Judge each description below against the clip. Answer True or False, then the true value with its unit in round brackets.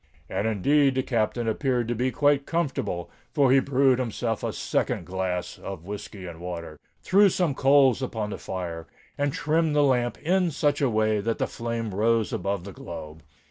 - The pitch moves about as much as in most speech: False (6.1 semitones)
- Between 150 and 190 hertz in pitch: False (120 Hz)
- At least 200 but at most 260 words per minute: False (175 wpm)